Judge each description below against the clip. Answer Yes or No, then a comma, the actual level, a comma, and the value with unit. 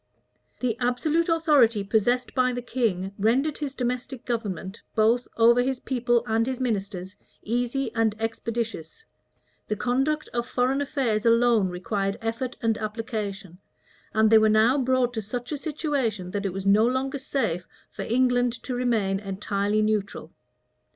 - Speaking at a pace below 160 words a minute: Yes, average, 150 wpm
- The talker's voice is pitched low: No, high, 230 Hz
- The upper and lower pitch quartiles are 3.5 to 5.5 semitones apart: No, average, 3.1 semitones